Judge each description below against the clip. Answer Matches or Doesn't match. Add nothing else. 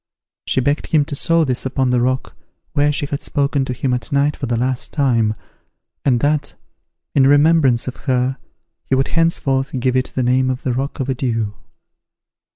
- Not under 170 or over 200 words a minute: Matches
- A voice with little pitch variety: Matches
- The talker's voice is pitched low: Matches